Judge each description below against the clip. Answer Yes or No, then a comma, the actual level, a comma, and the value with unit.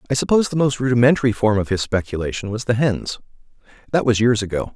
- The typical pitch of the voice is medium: No, low, 115 Hz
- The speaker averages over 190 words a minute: Yes, average, 200 wpm